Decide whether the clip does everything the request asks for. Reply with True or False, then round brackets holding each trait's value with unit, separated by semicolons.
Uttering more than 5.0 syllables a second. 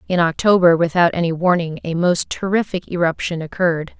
True (5.5 syllables/s)